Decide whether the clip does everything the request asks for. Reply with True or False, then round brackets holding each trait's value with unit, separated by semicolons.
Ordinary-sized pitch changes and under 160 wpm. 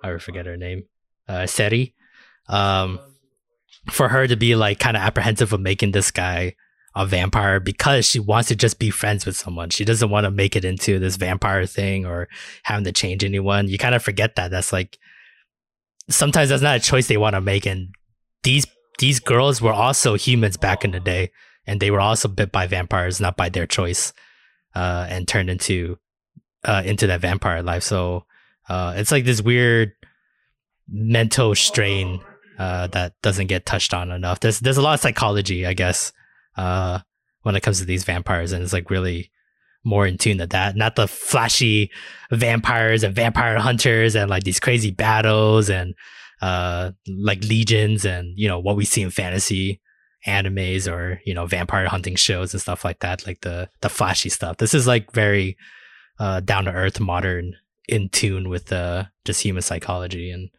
False (3.3 semitones; 185 wpm)